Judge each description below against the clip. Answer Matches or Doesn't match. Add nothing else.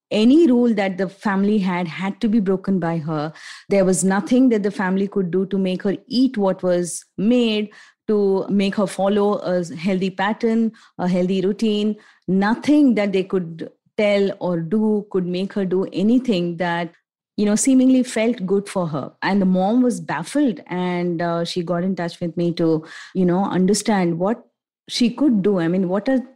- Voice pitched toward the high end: Matches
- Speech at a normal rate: Matches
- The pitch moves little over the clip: Doesn't match